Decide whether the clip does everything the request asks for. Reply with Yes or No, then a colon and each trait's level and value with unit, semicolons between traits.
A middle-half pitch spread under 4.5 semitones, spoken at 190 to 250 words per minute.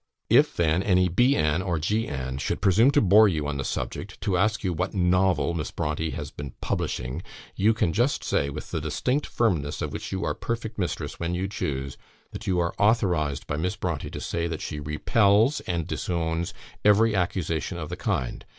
No: average, 4.9 semitones; average, 200 wpm